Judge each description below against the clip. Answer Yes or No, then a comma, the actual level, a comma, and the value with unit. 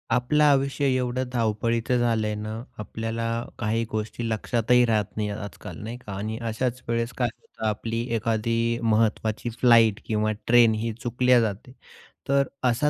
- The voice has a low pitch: Yes, low, 115 Hz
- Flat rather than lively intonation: Yes, narrow, 2.0 semitones